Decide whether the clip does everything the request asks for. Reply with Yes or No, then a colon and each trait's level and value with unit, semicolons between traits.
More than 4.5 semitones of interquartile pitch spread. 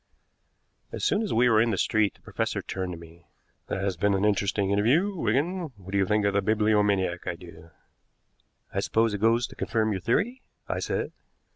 No: average, 3.3 semitones